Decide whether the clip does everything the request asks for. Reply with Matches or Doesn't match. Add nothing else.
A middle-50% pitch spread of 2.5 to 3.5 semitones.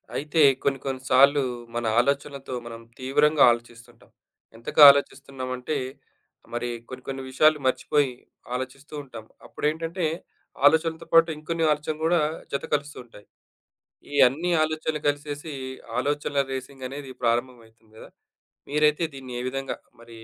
Matches